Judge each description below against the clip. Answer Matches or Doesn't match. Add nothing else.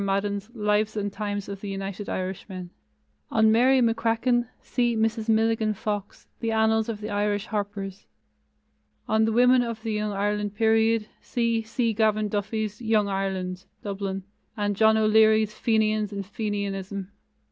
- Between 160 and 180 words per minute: Doesn't match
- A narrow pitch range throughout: Matches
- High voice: Matches